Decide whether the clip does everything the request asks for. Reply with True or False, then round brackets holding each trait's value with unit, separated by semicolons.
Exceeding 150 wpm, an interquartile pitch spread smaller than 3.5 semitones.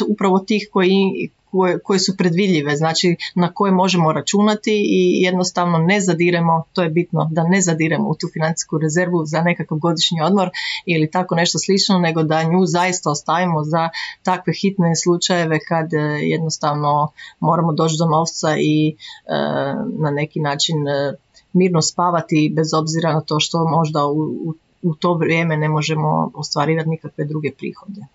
True (160 wpm; 2.6 semitones)